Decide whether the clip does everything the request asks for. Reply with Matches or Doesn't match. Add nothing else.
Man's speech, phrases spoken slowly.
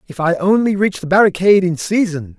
Doesn't match